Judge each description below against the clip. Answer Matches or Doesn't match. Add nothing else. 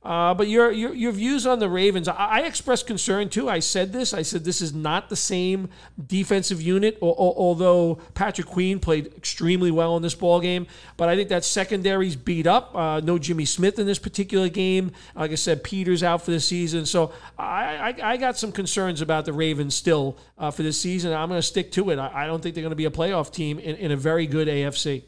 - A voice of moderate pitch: Matches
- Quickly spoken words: Matches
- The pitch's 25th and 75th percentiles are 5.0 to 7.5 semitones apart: Doesn't match